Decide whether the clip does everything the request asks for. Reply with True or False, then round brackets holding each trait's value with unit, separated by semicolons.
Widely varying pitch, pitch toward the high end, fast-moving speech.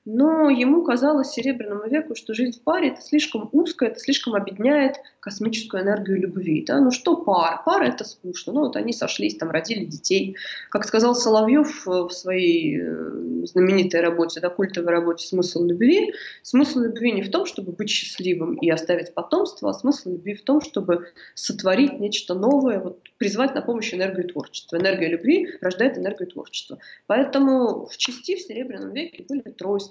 True (7.2 semitones; 220 Hz; 165 wpm)